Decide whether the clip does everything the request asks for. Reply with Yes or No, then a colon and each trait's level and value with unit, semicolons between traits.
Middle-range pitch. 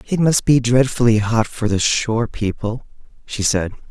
No: low, 115 Hz